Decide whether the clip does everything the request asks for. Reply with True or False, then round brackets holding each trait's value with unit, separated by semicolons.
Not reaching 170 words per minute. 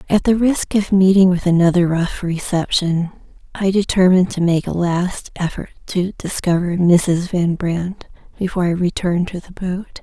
True (160 wpm)